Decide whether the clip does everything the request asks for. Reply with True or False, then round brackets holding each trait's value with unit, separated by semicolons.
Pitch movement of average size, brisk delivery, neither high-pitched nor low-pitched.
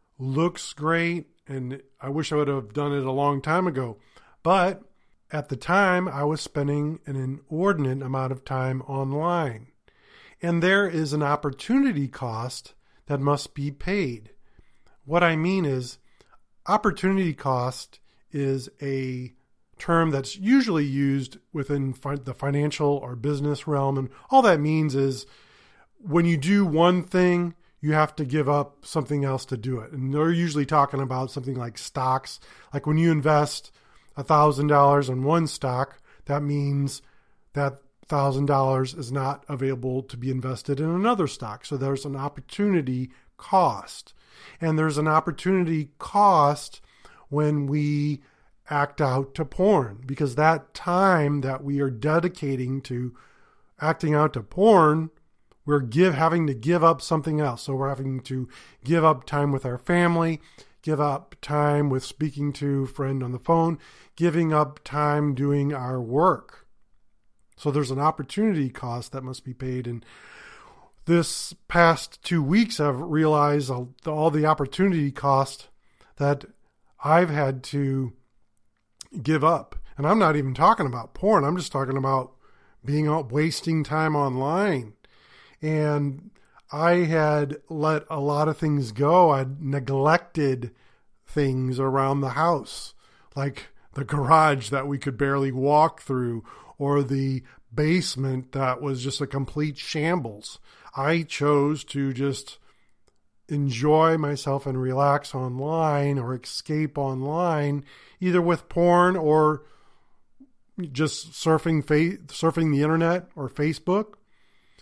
False (3.0 semitones; 140 wpm; 145 Hz)